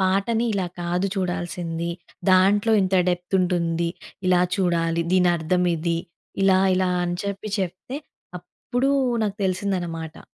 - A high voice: No, medium, 180 Hz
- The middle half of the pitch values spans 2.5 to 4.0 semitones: No, narrow, 2.0 semitones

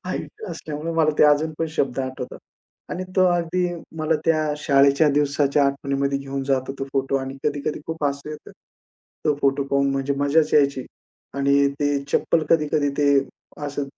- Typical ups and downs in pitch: No, narrow, 1.8 semitones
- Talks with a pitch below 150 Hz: Yes, medium, 140 Hz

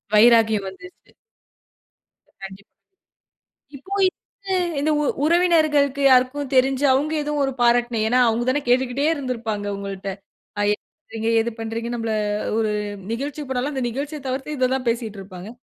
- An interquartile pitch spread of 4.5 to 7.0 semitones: No, average, 4.0 semitones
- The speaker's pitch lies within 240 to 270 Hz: Yes, very high, 250 Hz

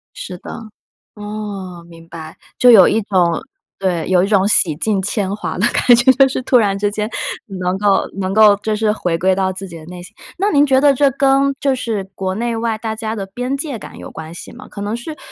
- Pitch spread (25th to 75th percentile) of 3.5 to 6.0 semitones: Yes, average, 4.2 semitones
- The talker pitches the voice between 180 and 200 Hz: No, high, 210 Hz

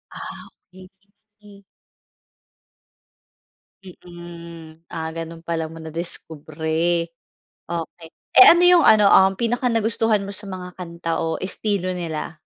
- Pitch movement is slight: No, average, 3.4 semitones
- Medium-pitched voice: Yes, medium, 175 Hz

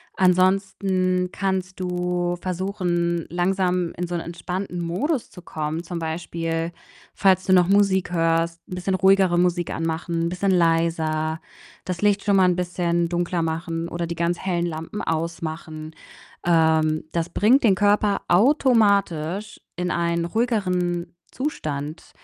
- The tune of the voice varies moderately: No, narrow, 2.2 semitones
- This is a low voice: No, medium, 175 Hz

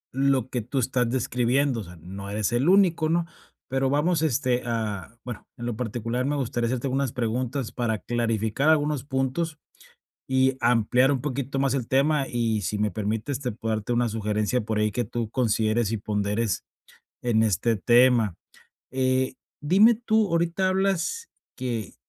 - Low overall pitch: Yes, low, 125 Hz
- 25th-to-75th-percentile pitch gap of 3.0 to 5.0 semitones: Yes, average, 3.7 semitones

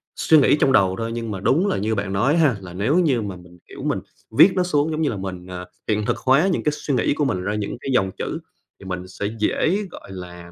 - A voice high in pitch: No, low, 105 Hz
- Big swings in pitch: Yes, wide, 7.6 semitones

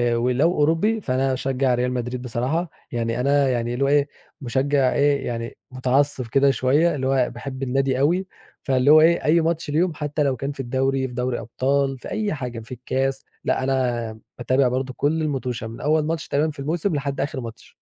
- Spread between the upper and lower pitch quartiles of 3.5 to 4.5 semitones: No, average, 2.7 semitones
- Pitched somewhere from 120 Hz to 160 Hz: Yes, low, 135 Hz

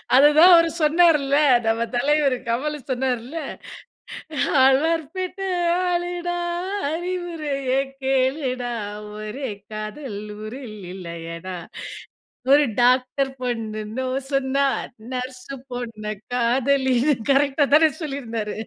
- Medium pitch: No, very high, 265 Hz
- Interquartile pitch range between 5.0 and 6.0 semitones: No, average, 3.8 semitones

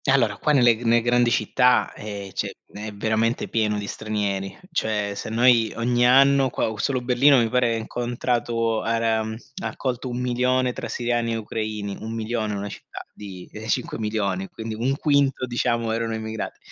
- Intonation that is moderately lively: No, narrow, 2.2 semitones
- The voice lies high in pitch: No, low, 115 Hz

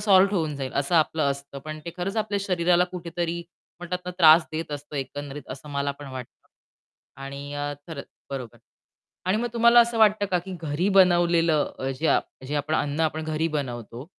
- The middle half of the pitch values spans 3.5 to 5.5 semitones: Yes, average, 4.1 semitones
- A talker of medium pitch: Yes, medium, 160 Hz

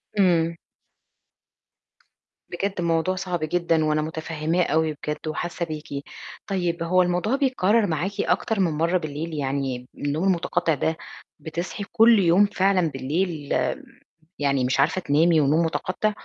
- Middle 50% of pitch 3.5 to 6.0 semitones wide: No, average, 3.1 semitones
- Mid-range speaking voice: Yes, medium, 165 Hz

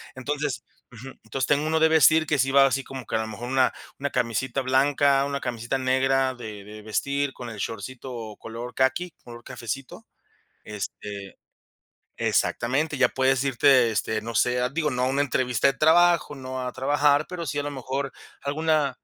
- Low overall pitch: Yes, low, 130 Hz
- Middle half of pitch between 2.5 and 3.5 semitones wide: Yes, average, 2.8 semitones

